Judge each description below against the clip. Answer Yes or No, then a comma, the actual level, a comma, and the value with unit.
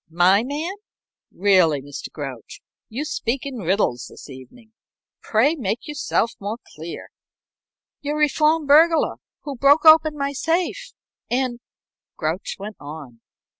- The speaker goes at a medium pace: No, slow, 130 wpm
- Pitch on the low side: No, high, 240 Hz